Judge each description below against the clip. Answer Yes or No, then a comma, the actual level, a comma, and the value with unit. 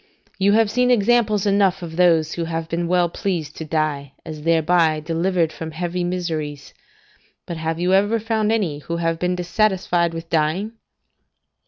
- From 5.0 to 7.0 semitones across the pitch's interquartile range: No, average, 3.2 semitones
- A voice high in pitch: No, medium, 170 Hz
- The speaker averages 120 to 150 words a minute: No, average, 165 wpm